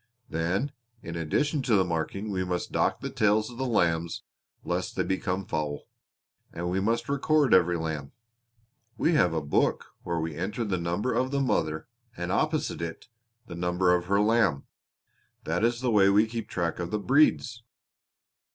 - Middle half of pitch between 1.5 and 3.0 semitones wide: No, wide, 5.5 semitones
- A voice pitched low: Yes, very low, 95 Hz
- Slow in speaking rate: No, average, 175 wpm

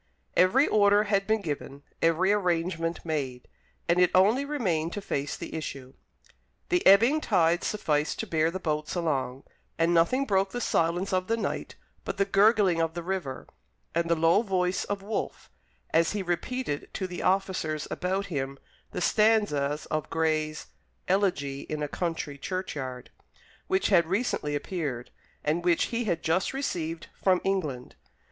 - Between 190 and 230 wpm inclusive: No, average, 155 wpm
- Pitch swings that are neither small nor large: Yes, average, 4.1 semitones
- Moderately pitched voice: Yes, medium, 175 Hz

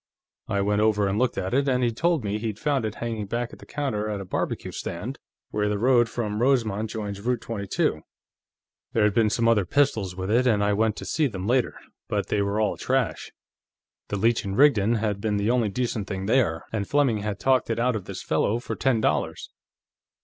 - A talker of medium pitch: No, low, 110 Hz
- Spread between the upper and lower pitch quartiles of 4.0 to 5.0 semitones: No, average, 3.2 semitones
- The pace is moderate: No, fast, 220 wpm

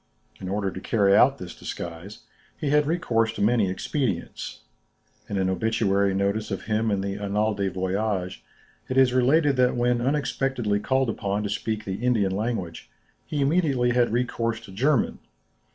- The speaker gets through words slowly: No, average, 165 wpm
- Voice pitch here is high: No, low, 110 Hz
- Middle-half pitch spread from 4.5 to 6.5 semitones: No, average, 4.1 semitones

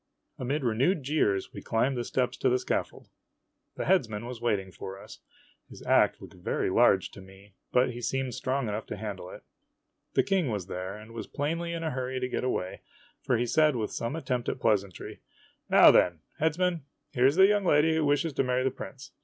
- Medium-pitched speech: No, low, 125 Hz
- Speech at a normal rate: No, fast, 210 wpm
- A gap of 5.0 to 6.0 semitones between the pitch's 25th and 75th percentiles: Yes, wide, 5.5 semitones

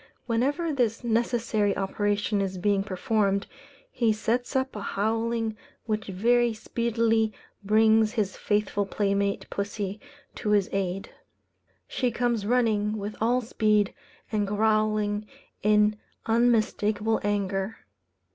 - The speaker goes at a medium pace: No, slow, 110 wpm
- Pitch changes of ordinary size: No, narrow, 2.0 semitones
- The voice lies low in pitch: No, high, 215 Hz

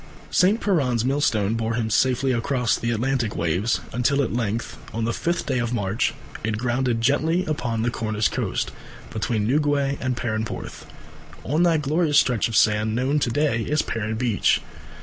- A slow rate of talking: No, average, 170 wpm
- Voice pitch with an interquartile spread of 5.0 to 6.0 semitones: No, average, 3.9 semitones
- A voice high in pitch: No, low, 120 Hz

